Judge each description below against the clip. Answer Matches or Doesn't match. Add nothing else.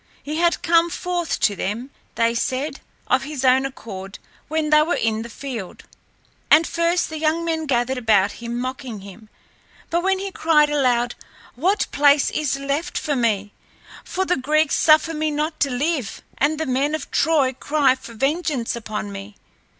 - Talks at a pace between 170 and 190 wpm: Matches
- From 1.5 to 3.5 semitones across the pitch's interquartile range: Doesn't match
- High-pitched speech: Matches